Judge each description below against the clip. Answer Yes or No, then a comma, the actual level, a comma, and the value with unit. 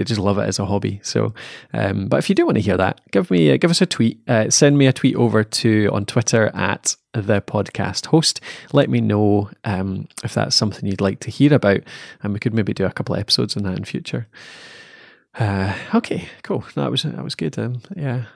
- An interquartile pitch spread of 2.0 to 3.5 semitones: No, wide, 5.4 semitones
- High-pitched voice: No, low, 115 Hz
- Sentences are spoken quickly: Yes, fast, 240 wpm